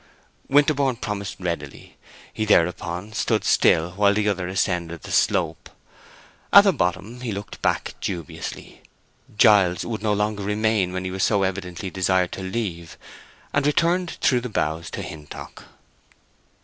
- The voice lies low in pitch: Yes, low, 100 Hz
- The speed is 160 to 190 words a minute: No, average, 145 wpm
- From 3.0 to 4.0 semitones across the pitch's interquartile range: Yes, average, 3.6 semitones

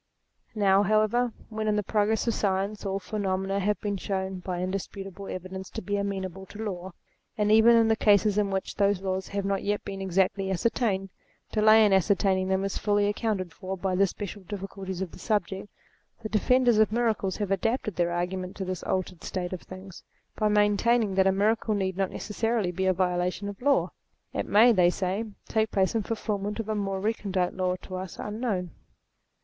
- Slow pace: No, average, 190 wpm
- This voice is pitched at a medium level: No, high, 195 Hz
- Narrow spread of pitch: Yes, narrow, 2.1 semitones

